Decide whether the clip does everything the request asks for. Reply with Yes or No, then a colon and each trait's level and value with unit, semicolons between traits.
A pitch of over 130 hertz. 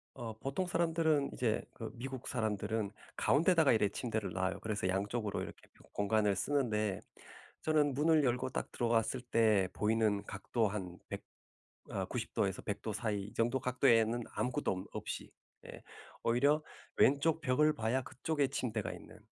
No: low, 115 Hz